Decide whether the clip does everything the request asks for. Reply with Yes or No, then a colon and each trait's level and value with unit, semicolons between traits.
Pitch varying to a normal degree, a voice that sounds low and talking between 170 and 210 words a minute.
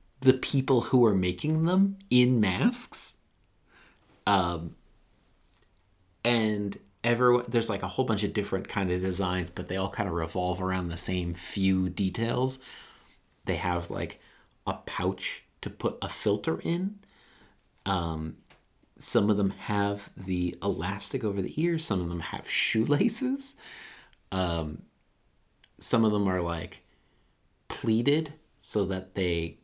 No: average, 4.9 semitones; low, 100 Hz; slow, 135 wpm